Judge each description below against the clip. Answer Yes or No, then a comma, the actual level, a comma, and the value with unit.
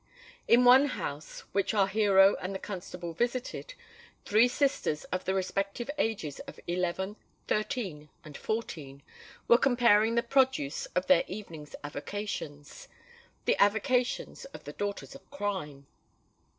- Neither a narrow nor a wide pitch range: No, wide, 5.7 semitones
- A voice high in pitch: Yes, high, 200 Hz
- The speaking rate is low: Yes, slow, 125 wpm